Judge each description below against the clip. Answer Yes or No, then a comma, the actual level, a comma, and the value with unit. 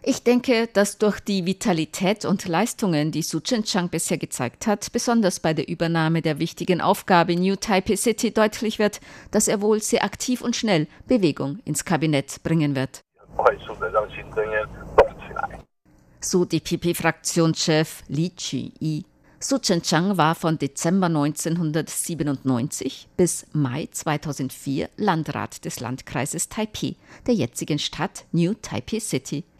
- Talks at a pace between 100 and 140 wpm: Yes, average, 135 wpm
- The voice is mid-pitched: Yes, medium, 170 Hz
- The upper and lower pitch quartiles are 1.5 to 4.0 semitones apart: No, average, 4.7 semitones